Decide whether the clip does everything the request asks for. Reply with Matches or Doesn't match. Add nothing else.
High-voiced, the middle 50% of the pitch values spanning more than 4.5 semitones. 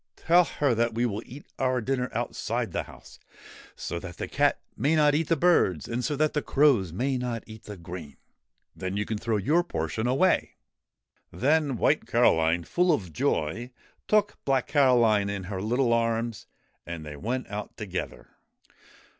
Doesn't match